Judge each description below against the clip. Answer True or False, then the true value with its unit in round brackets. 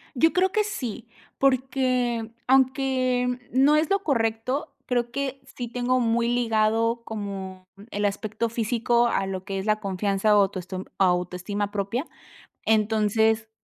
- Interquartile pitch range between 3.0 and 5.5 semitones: True (3.7 semitones)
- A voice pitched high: True (230 Hz)